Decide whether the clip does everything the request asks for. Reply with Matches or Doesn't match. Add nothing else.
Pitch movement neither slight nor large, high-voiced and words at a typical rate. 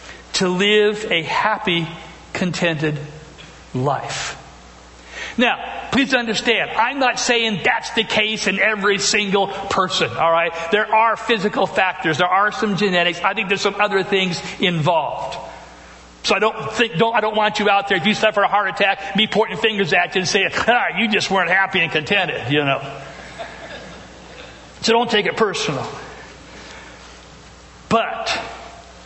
Matches